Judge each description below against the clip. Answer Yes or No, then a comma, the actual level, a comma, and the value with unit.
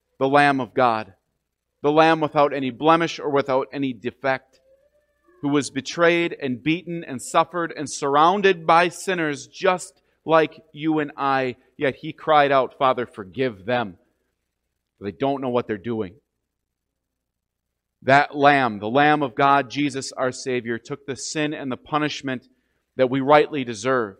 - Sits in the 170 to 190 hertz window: No, medium, 140 Hz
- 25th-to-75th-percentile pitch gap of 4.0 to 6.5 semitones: No, average, 3.5 semitones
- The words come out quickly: No, average, 150 wpm